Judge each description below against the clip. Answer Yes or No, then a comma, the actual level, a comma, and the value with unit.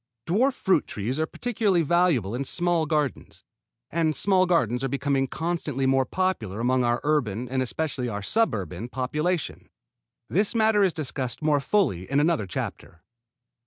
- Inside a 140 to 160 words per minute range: Yes, average, 150 wpm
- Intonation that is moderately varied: No, wide, 5.8 semitones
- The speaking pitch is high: No, medium, 145 Hz